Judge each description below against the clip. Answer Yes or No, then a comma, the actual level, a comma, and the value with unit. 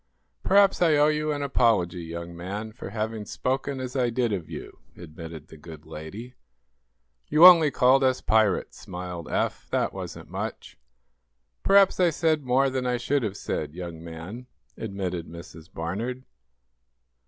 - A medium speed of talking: Yes, average, 155 wpm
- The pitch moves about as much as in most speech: No, wide, 7.6 semitones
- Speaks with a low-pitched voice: Yes, low, 110 Hz